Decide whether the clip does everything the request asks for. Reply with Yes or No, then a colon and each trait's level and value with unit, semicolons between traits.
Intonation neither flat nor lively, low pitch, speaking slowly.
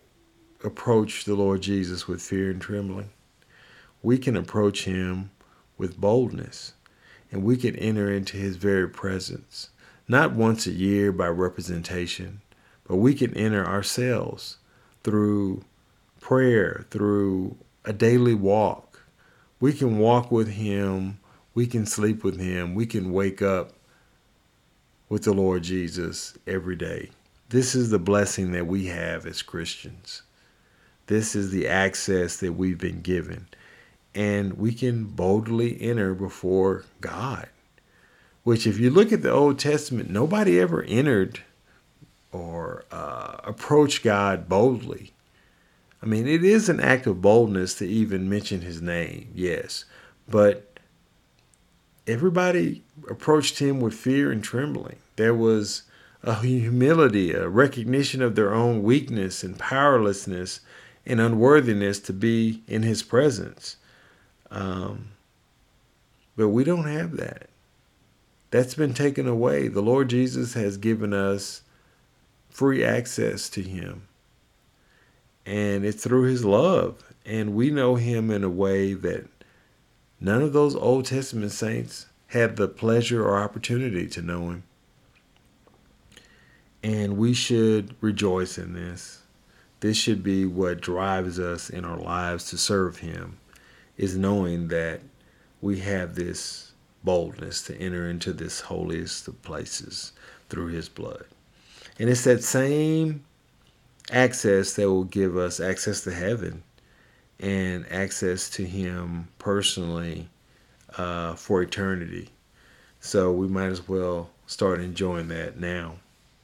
Yes: average, 4.1 semitones; low, 100 Hz; slow, 130 wpm